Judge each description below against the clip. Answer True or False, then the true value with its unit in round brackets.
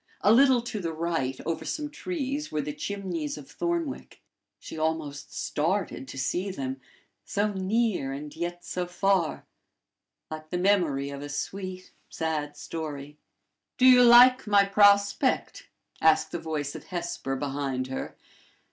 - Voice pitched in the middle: True (170 Hz)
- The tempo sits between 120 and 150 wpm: True (145 wpm)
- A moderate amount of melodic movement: False (5.7 semitones)